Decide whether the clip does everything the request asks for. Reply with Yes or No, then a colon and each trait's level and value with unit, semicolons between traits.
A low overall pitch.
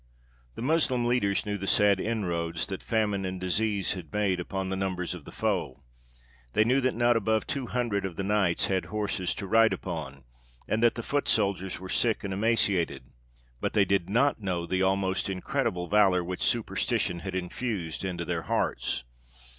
Yes: very low, 95 Hz